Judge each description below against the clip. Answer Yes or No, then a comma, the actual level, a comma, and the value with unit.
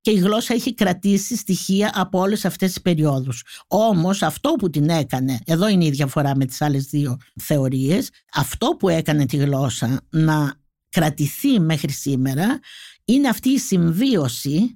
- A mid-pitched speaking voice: Yes, medium, 165 Hz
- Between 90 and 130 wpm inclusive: No, average, 155 wpm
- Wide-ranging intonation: Yes, wide, 6.0 semitones